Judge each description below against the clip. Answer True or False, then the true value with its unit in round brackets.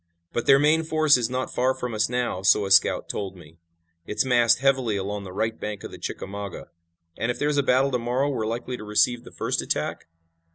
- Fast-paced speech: True (220 wpm)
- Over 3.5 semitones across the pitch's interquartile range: True (4.0 semitones)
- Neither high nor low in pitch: False (120 Hz)